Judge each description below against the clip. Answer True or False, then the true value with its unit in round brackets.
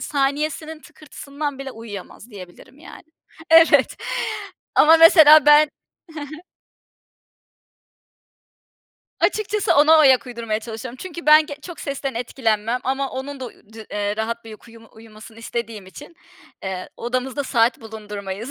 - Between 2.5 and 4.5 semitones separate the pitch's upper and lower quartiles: False (5.1 semitones)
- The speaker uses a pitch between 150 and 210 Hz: False (255 Hz)